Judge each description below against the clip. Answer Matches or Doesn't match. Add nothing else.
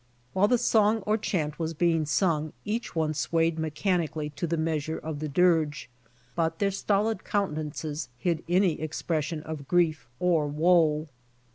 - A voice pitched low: Doesn't match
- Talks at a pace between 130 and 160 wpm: Matches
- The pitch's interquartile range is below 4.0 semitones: Matches